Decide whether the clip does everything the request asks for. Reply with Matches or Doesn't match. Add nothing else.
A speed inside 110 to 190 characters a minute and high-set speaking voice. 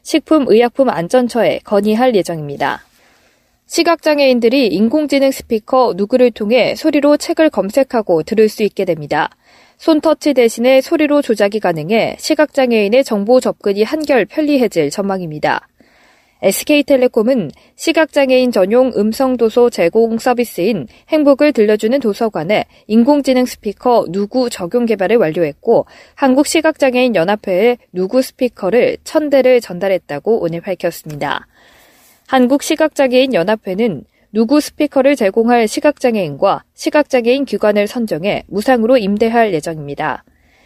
Doesn't match